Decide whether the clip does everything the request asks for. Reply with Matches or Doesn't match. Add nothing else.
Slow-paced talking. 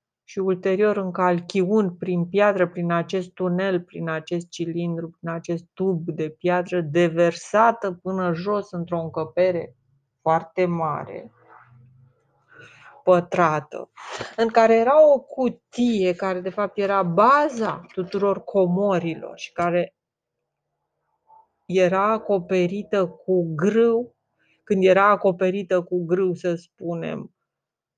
Matches